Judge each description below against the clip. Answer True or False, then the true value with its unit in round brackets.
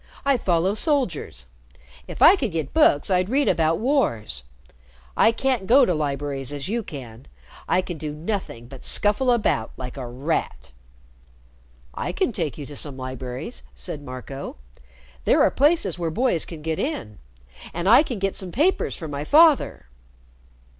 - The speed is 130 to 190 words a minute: True (160 wpm)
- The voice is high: False (165 Hz)